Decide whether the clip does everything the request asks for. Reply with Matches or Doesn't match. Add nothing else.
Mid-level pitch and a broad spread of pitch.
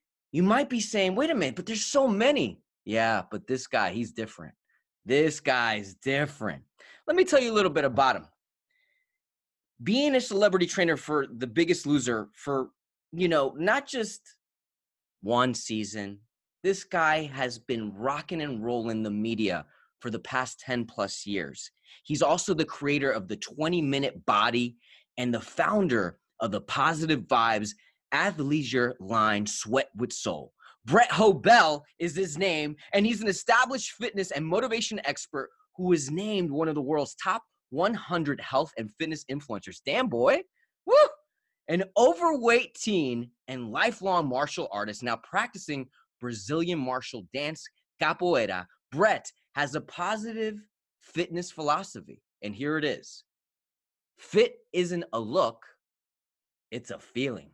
Matches